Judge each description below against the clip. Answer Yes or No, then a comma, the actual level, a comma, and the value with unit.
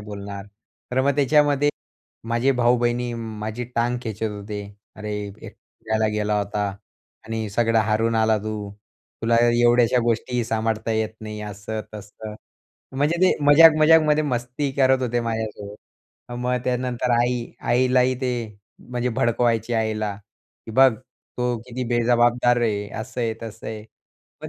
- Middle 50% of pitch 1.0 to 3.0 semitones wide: Yes, narrow, 2.5 semitones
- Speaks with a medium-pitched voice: No, low, 115 Hz